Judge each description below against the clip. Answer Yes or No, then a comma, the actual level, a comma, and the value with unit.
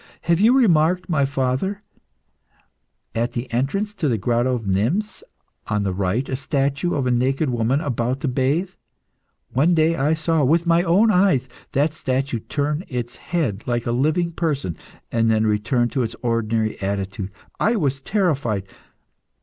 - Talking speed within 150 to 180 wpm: Yes, average, 160 wpm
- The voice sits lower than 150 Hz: Yes, low, 135 Hz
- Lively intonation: Yes, wide, 5.8 semitones